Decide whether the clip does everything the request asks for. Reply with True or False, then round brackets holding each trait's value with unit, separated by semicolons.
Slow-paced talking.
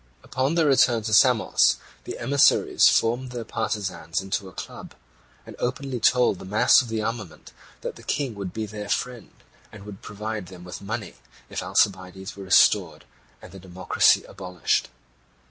False (165 wpm)